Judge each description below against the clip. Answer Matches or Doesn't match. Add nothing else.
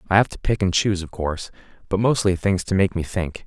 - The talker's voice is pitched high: Doesn't match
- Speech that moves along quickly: Matches